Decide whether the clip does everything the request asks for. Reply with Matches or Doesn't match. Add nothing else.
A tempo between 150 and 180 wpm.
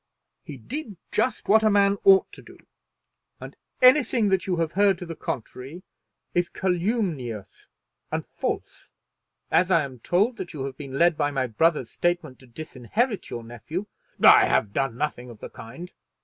Matches